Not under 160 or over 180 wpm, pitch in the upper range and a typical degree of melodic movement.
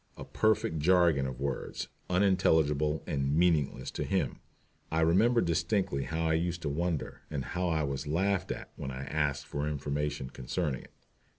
No: average, 165 wpm; very low, 80 Hz; average, 3.7 semitones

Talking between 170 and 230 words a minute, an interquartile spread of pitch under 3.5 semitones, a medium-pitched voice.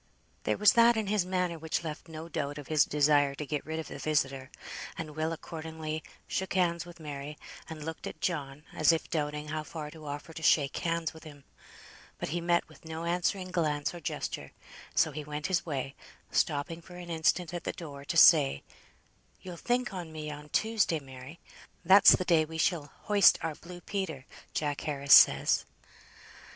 Yes: average, 190 wpm; average, 2.7 semitones; medium, 160 Hz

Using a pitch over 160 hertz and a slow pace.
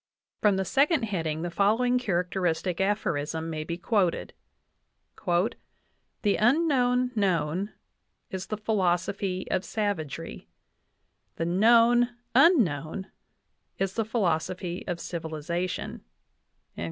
Yes: high, 190 Hz; slow, 100 wpm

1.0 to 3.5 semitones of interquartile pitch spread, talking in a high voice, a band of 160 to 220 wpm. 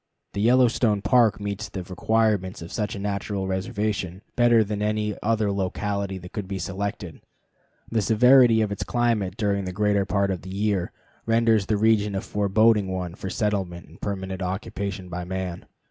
No: narrow, 2.4 semitones; low, 100 Hz; average, 170 wpm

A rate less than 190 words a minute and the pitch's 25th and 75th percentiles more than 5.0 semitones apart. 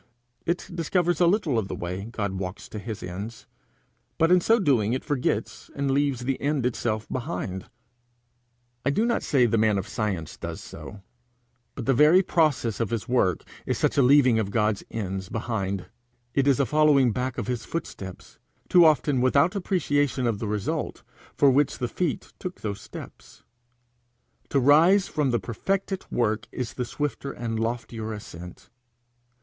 Yes: average, 170 wpm; wide, 5.4 semitones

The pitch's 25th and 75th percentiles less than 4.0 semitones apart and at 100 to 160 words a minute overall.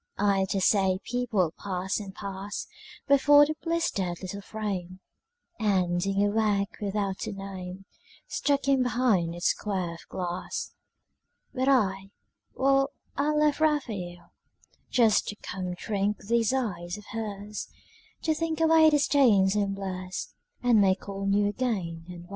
No: average, 4.7 semitones; average, 140 wpm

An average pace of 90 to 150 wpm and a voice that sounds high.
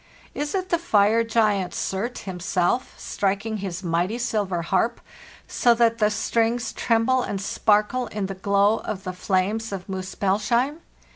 Yes: average, 145 wpm; high, 210 Hz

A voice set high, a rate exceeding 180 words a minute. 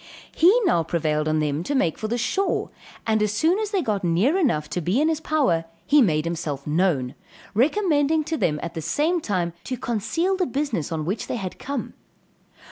Yes: high, 220 Hz; average, 200 wpm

